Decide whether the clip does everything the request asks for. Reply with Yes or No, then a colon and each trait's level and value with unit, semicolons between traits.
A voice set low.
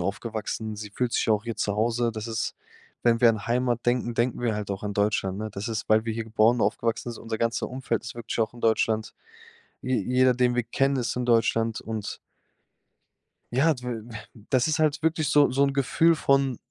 Yes: low, 115 Hz